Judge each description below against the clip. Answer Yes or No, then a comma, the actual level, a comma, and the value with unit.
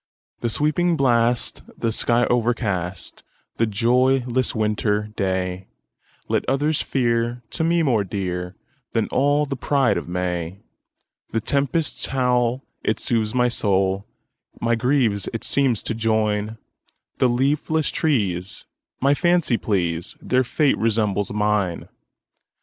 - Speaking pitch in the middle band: No, low, 115 Hz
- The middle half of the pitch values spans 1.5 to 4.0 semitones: No, average, 4.4 semitones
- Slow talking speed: Yes, slow, 105 wpm